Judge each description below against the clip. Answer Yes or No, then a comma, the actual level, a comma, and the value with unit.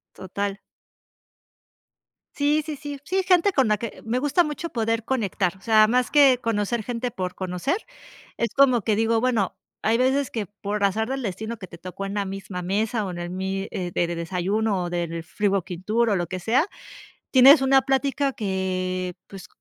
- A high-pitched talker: Yes, high, 215 Hz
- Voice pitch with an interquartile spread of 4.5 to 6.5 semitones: Yes, average, 5.2 semitones